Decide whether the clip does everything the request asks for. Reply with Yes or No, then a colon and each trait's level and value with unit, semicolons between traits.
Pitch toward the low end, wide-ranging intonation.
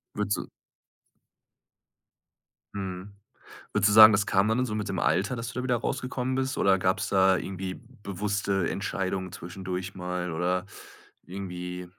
No: very low, 95 Hz; narrow, 2.5 semitones